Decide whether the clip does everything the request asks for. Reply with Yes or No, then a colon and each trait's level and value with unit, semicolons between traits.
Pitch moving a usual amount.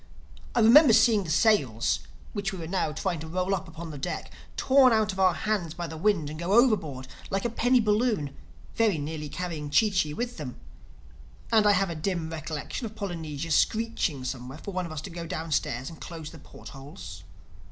No: wide, 5.7 semitones